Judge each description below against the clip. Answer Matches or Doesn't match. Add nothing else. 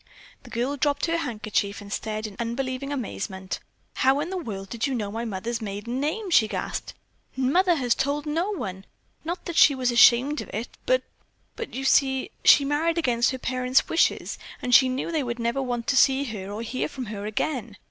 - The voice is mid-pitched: Doesn't match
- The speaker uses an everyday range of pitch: Matches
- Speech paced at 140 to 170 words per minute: Doesn't match